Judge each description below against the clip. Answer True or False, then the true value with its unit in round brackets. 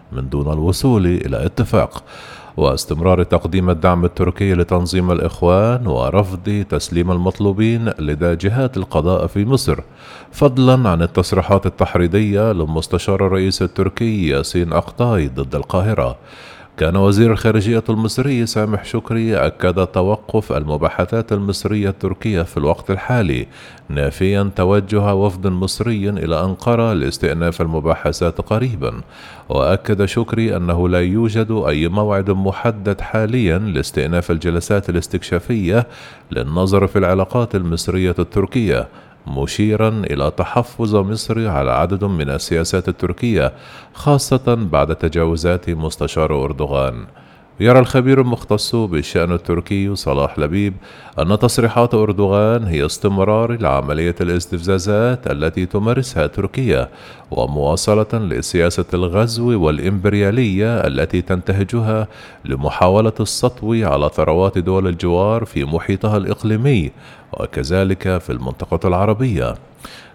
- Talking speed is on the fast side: False (105 wpm)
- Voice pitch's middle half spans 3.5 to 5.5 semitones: True (4.0 semitones)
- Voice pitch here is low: True (95 Hz)